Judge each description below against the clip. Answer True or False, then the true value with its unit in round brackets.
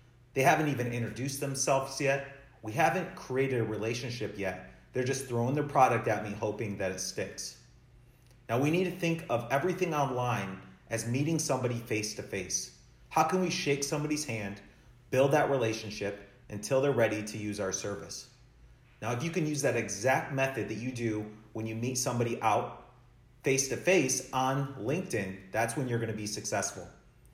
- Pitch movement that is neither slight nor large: True (3.8 semitones)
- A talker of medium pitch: False (125 Hz)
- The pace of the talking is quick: False (180 wpm)